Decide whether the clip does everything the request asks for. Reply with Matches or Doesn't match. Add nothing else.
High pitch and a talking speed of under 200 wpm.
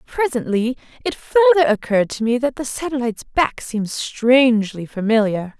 Matches